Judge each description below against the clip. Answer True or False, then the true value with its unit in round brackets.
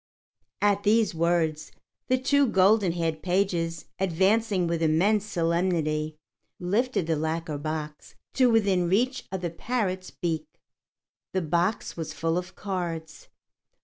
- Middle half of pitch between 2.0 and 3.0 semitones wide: False (3.8 semitones)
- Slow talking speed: True (125 wpm)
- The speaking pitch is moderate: True (175 Hz)